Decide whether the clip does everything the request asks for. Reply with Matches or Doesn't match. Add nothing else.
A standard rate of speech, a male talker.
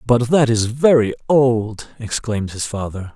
Matches